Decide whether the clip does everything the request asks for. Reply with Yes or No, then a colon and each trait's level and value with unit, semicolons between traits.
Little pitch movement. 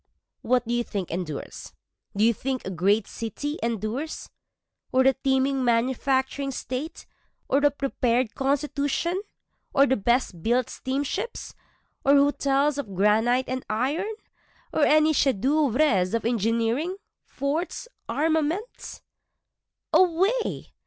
No: average, 3.8 semitones